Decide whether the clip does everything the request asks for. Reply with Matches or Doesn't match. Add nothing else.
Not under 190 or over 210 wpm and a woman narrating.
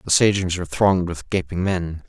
Doesn't match